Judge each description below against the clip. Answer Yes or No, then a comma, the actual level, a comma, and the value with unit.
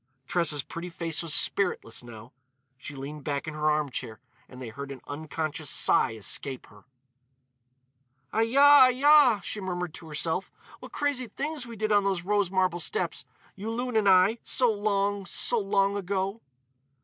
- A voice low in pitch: No, medium, 185 Hz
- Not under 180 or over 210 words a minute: No, average, 160 wpm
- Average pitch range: No, wide, 6.3 semitones